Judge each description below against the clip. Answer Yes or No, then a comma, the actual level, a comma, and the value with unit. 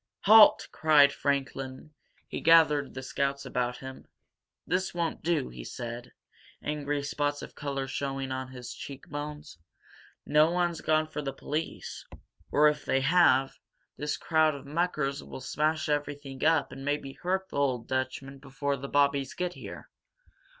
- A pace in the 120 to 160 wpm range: Yes, average, 150 wpm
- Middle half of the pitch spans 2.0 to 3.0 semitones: Yes, narrow, 2.4 semitones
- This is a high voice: No, medium, 145 Hz